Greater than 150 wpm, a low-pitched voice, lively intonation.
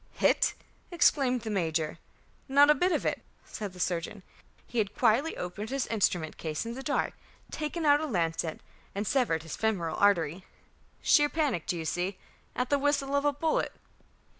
No: average, 175 wpm; high, 220 Hz; wide, 8.2 semitones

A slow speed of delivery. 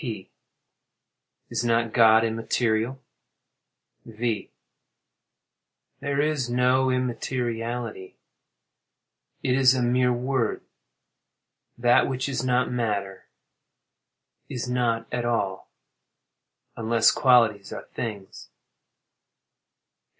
Yes: slow, 75 wpm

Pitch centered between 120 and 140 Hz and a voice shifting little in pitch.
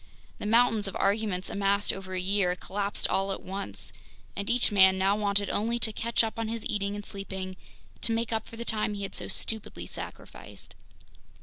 No: high, 205 Hz; narrow, 2.3 semitones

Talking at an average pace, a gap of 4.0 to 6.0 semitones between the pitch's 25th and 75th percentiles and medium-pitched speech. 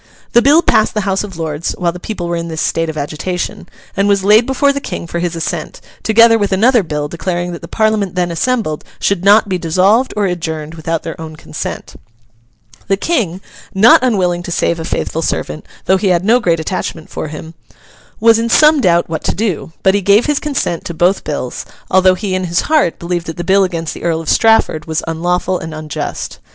No: fast, 210 wpm; average, 4.3 semitones; medium, 180 Hz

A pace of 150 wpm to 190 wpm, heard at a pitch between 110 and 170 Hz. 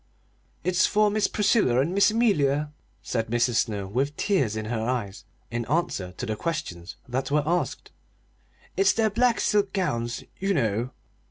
Yes: average, 160 wpm; medium, 140 Hz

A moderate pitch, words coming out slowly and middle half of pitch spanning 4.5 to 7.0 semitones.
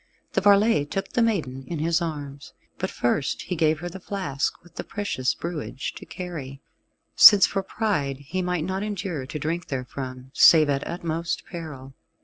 No: medium, 160 Hz; average, 170 wpm; average, 5.1 semitones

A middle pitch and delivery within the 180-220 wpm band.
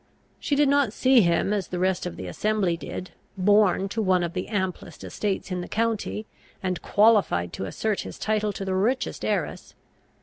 No: high, 200 Hz; average, 190 wpm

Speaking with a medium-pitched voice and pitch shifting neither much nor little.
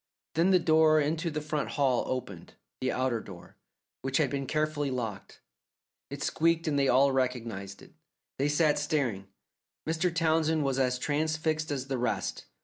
Yes: medium, 145 Hz; average, 3.6 semitones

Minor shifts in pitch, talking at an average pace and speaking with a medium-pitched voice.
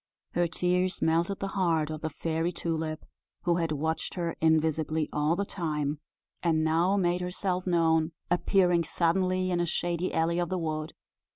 Yes: narrow, 2.0 semitones; average, 165 wpm; medium, 170 Hz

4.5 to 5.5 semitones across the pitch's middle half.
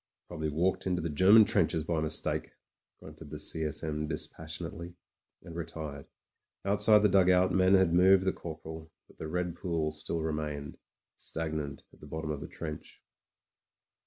No: average, 2.7 semitones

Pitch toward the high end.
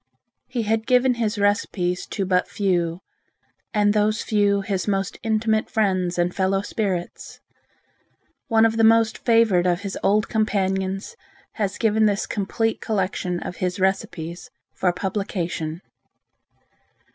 Yes: high, 200 Hz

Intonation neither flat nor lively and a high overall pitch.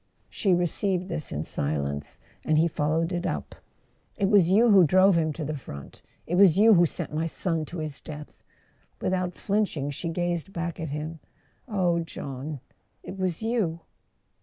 No: average, 3.5 semitones; medium, 170 Hz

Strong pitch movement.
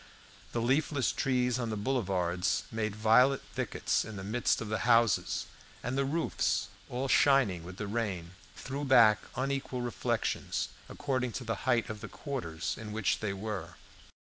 No: average, 4.0 semitones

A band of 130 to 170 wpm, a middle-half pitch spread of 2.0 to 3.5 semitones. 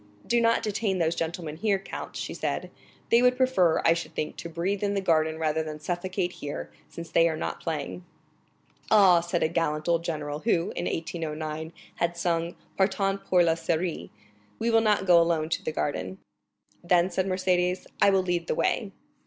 No: average, 185 wpm; average, 3.0 semitones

